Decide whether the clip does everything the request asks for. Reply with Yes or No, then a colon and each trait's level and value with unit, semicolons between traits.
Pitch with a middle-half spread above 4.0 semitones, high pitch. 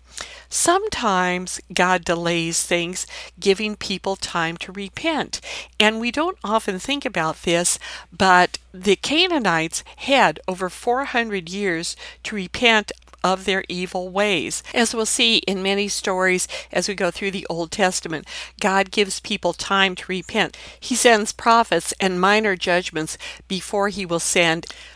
No: average, 3.0 semitones; high, 195 Hz